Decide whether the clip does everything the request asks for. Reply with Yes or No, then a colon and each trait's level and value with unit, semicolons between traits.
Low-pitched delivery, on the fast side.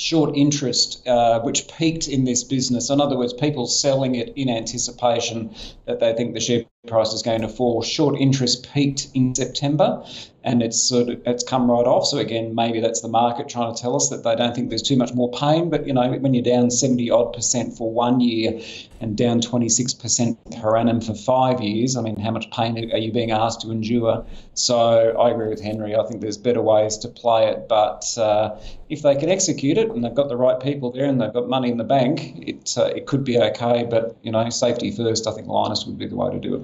Yes: low, 120 Hz; fast, 235 wpm